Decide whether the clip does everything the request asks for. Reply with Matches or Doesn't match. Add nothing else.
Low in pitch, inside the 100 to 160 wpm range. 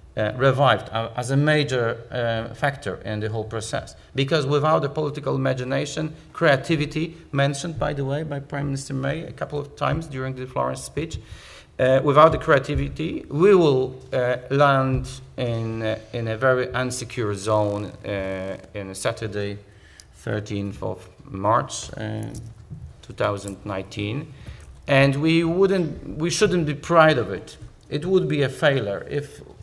Matches